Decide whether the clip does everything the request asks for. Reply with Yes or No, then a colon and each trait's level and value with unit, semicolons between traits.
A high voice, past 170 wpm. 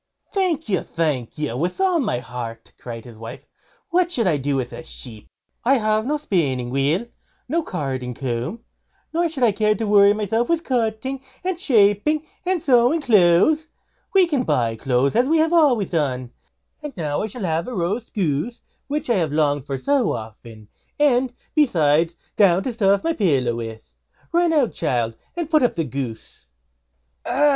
Yes: high, 200 Hz; average, 180 wpm